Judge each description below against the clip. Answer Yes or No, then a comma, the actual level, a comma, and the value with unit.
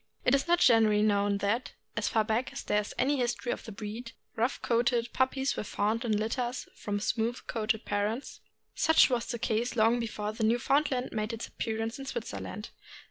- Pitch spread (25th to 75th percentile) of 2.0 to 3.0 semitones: Yes, narrow, 2.5 semitones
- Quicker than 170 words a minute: Yes, average, 190 wpm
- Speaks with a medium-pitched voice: No, high, 230 Hz